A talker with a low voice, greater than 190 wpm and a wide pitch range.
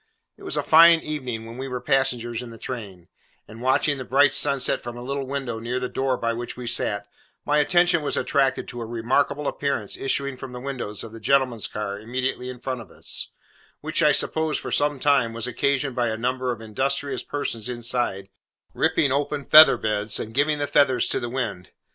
No: low, 125 Hz; fast, 205 wpm; average, 3.3 semitones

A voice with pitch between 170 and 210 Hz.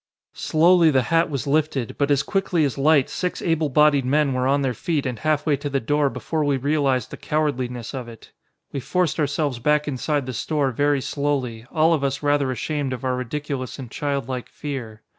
No: medium, 140 Hz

